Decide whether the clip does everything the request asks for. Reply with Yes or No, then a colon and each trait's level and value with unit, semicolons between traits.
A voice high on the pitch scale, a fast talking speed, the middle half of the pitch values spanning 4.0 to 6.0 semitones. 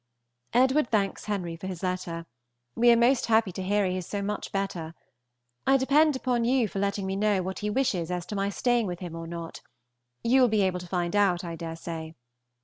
Yes: high, 195 Hz; fast, 220 wpm; average, 4.8 semitones